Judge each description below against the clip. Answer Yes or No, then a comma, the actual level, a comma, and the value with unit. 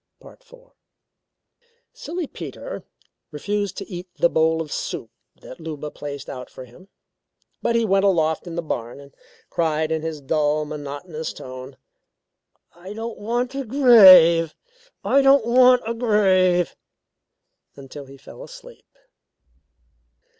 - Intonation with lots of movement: Yes, wide, 6.5 semitones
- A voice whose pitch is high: No, medium, 170 Hz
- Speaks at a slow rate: Yes, slow, 130 wpm